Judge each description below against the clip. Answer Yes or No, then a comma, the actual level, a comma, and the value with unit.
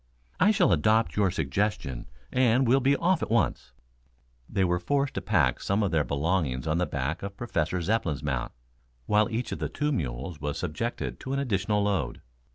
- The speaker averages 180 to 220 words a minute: Yes, average, 185 wpm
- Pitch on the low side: Yes, low, 100 Hz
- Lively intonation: Yes, wide, 7.2 semitones